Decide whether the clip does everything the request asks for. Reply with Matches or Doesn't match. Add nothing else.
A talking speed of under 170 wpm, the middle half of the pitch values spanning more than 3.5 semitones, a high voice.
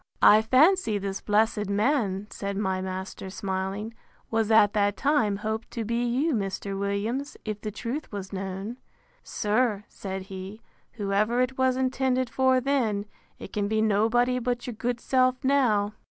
Matches